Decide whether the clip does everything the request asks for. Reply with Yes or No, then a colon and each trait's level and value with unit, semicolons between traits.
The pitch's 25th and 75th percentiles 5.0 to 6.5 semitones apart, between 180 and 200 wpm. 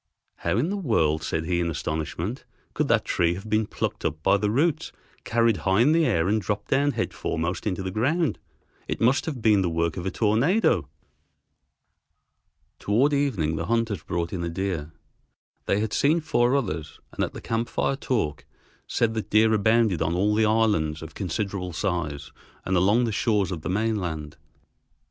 Yes: average, 5.3 semitones; average, 185 wpm